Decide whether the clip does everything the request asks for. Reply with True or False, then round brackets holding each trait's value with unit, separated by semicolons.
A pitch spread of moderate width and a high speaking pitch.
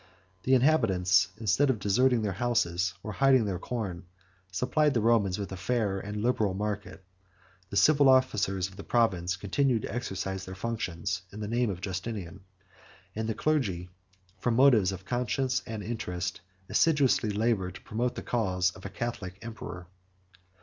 False (4.5 semitones; 105 Hz)